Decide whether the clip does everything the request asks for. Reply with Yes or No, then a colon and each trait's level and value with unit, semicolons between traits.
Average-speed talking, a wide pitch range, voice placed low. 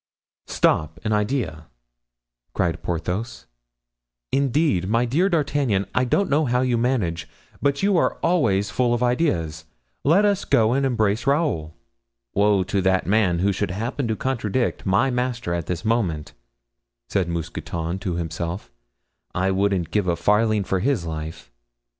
Yes: average, 145 wpm; wide, 6.2 semitones; low, 105 Hz